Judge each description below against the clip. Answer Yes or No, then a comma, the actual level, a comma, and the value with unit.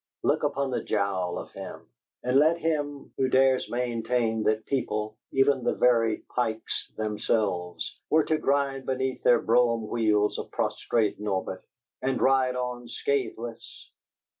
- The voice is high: No, low, 120 Hz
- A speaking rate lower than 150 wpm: Yes, average, 140 wpm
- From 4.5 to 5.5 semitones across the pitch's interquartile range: No, average, 3.5 semitones